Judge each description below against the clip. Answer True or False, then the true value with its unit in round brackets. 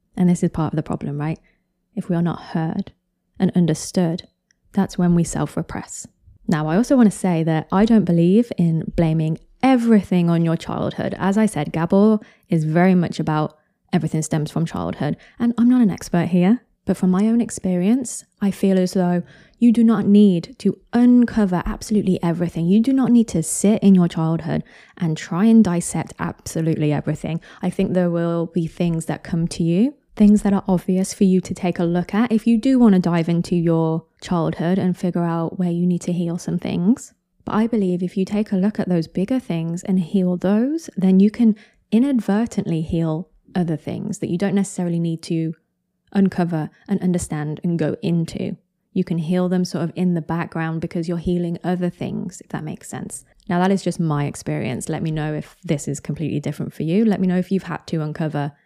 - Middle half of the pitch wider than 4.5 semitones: False (3.3 semitones)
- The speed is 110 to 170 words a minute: False (205 wpm)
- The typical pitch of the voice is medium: True (180 Hz)